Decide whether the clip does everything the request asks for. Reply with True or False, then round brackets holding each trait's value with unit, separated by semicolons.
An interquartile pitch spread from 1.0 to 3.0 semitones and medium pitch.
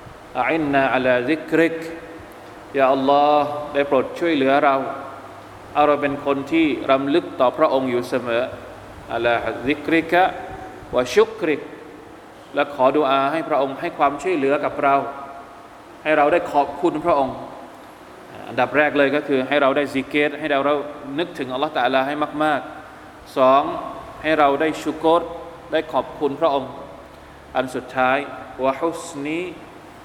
True (2.7 semitones; 145 Hz)